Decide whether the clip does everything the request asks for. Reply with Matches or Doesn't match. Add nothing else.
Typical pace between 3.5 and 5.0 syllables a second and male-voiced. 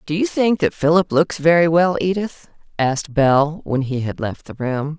Doesn't match